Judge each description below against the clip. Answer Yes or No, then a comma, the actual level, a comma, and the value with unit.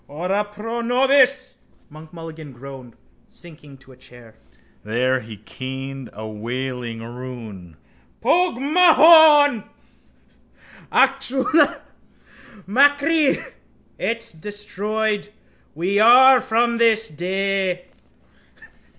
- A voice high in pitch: Yes, high, 195 Hz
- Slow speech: Yes, slow, 85 wpm